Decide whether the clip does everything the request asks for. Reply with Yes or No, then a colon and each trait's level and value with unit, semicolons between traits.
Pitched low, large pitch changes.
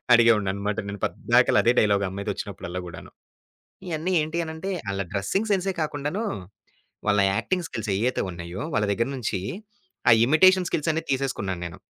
Yes: low, 115 Hz; wide, 8.2 semitones